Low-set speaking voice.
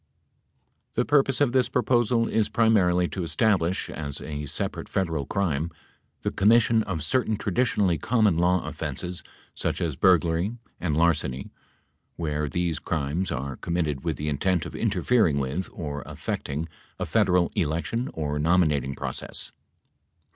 Yes: very low, 85 Hz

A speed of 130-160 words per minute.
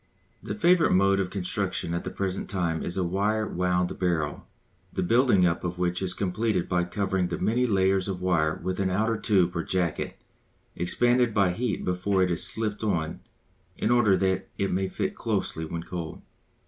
No: average, 185 wpm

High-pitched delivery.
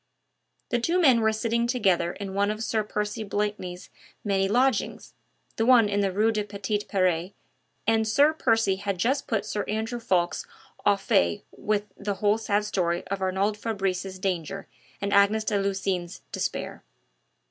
Yes: high, 205 Hz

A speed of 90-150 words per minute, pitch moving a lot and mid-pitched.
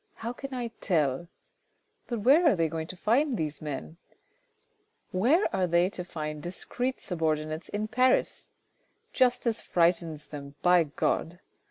Yes: average, 140 wpm; wide, 7.2 semitones; medium, 180 Hz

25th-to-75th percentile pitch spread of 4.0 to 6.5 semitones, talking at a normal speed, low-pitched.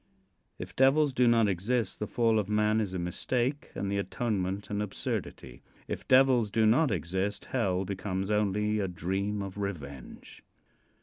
No: average, 3.3 semitones; average, 160 wpm; low, 105 Hz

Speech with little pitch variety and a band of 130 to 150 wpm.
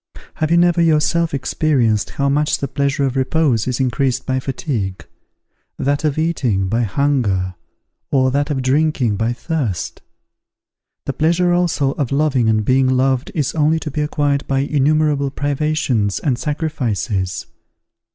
No: average, 3.5 semitones; average, 145 wpm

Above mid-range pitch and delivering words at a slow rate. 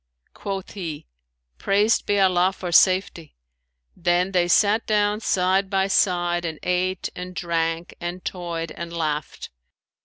No: medium, 180 Hz; slow, 130 wpm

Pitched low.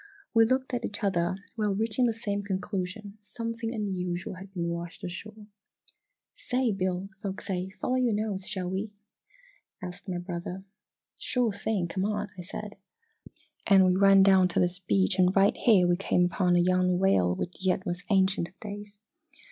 No: high, 195 Hz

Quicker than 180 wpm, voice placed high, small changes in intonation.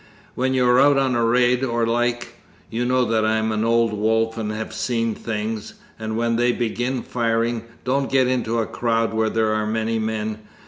No: average, 195 wpm; low, 115 Hz; narrow, 1.7 semitones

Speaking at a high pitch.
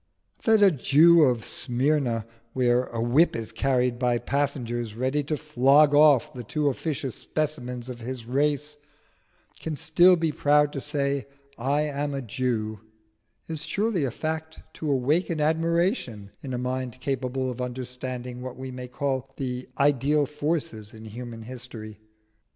No: low, 135 Hz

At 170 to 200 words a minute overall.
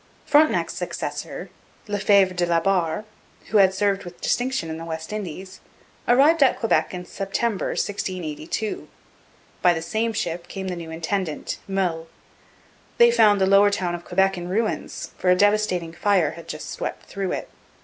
No: average, 160 wpm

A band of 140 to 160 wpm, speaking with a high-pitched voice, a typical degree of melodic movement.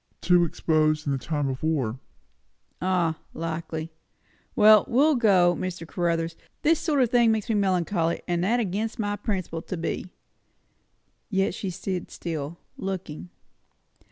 No: average, 145 wpm; medium, 175 Hz; average, 4.0 semitones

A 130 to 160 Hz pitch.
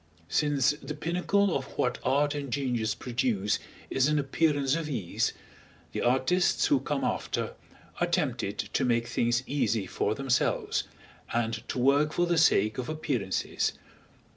Yes: low, 135 Hz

